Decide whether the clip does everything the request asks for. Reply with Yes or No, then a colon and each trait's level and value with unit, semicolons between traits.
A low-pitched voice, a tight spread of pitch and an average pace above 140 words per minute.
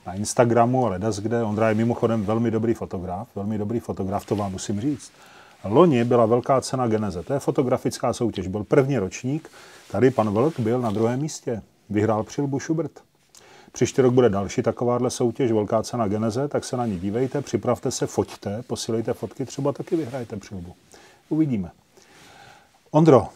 No: low, 115 Hz; average, 3.4 semitones; average, 165 wpm